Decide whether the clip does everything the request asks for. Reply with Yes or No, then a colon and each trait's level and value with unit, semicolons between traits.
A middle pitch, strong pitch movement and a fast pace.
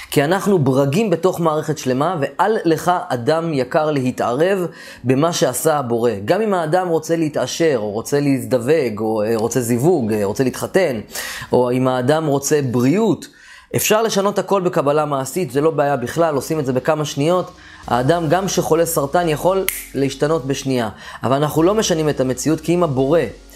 No: medium, 155 Hz; average, 4.6 semitones; fast, 160 wpm